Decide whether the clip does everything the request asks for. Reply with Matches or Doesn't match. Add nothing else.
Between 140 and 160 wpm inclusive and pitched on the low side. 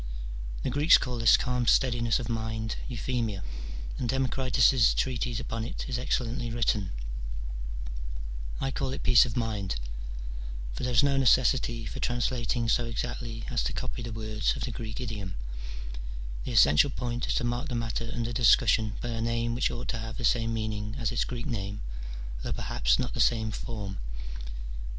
Doesn't match